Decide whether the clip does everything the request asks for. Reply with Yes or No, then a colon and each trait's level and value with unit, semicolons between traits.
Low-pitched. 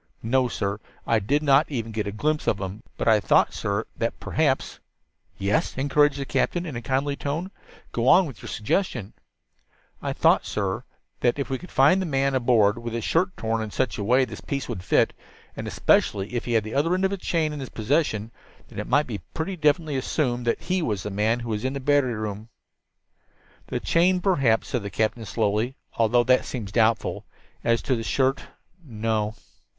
Yes: low, 125 Hz